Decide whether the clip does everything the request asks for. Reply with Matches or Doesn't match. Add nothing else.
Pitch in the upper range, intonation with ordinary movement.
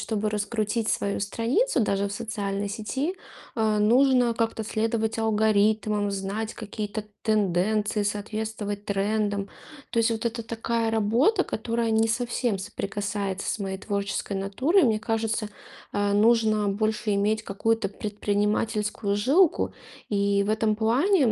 Doesn't match